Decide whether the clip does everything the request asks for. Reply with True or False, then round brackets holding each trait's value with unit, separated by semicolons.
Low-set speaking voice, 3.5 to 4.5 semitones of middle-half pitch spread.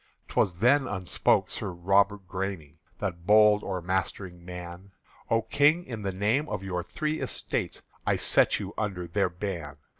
False (95 Hz; 3.1 semitones)